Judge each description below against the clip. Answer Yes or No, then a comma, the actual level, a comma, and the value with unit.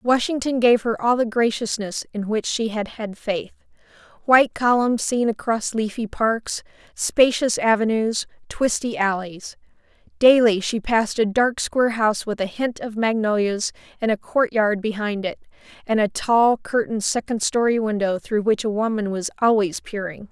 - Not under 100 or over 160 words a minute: Yes, average, 155 wpm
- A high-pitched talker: Yes, high, 220 Hz